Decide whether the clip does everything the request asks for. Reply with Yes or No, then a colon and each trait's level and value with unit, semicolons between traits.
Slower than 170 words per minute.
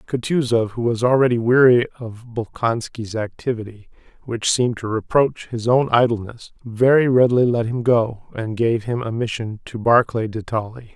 Yes: average, 160 wpm